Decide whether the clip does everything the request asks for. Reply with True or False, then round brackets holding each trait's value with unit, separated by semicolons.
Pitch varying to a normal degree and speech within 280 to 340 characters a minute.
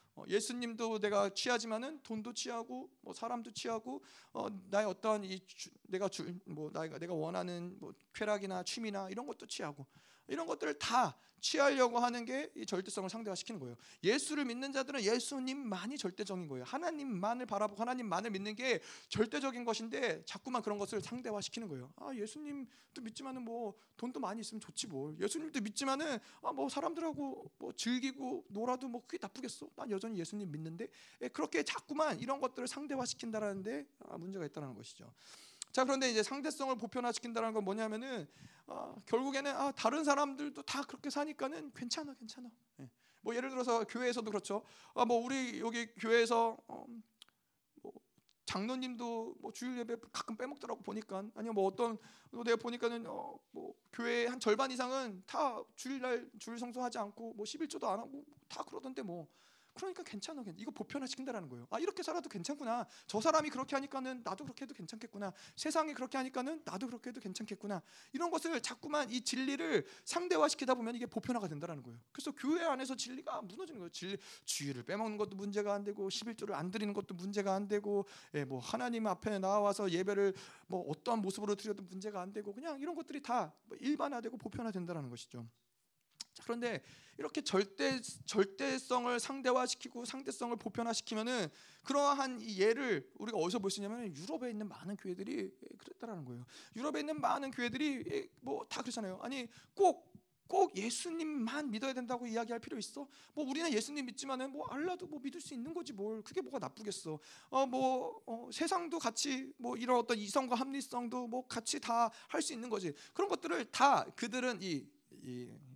False (4.6 semitones; 395 characters per minute)